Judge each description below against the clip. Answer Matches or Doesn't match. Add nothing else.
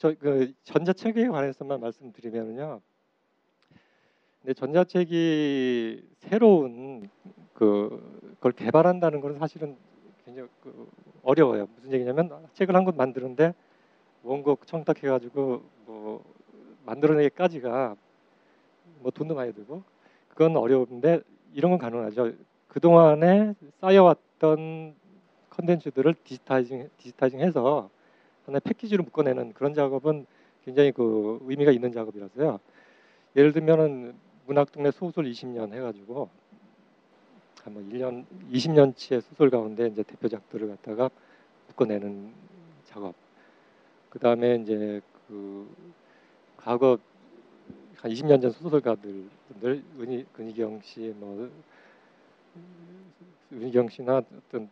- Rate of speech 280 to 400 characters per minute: Doesn't match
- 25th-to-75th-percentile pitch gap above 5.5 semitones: Doesn't match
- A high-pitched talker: Doesn't match